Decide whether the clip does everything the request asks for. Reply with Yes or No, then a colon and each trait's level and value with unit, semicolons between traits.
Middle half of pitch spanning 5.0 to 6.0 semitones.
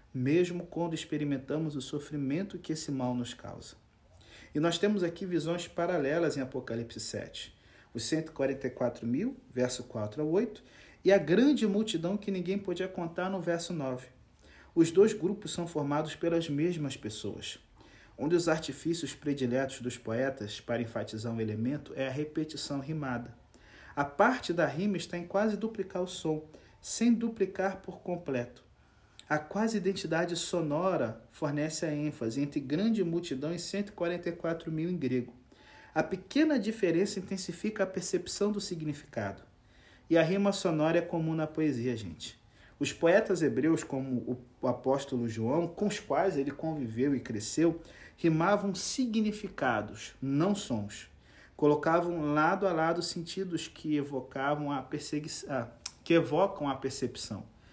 Yes: wide, 5.4 semitones